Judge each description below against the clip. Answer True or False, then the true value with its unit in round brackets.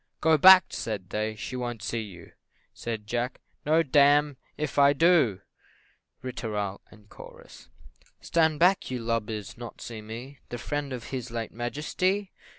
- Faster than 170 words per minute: False (150 wpm)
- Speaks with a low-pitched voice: True (120 Hz)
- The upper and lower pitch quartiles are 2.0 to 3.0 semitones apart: False (5.1 semitones)